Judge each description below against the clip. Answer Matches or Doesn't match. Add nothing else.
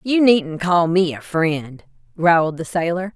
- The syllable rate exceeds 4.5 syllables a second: Doesn't match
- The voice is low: Doesn't match